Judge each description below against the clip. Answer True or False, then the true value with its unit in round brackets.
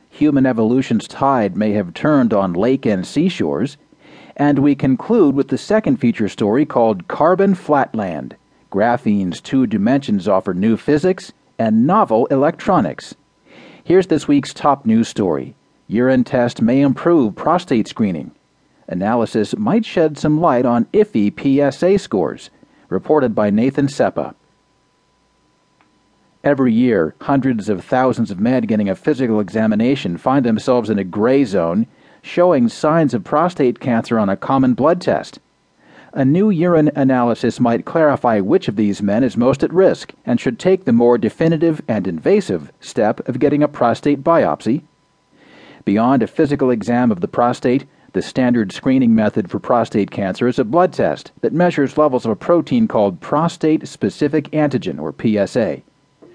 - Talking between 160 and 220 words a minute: False (150 wpm)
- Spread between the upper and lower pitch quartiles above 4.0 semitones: True (5.1 semitones)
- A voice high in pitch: False (135 Hz)